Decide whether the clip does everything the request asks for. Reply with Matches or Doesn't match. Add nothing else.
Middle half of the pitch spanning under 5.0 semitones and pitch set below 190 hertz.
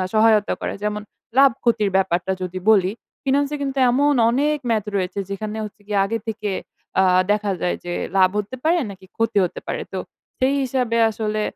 Doesn't match